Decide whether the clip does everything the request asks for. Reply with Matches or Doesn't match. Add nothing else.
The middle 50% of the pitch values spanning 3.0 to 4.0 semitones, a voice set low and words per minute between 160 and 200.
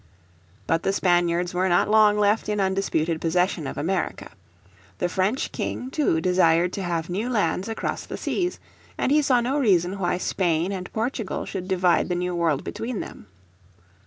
Doesn't match